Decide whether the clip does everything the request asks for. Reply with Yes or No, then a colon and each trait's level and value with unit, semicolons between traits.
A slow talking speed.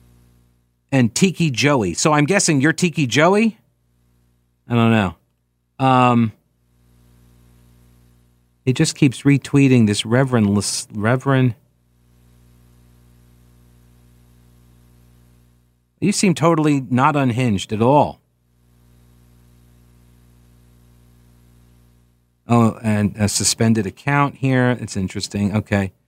Yes: slow, 80 wpm